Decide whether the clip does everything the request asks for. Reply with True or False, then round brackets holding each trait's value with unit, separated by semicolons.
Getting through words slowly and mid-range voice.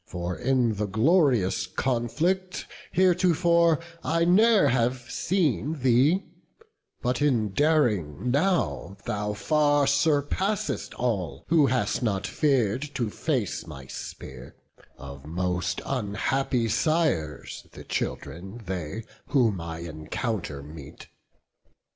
False (105 wpm; 120 Hz)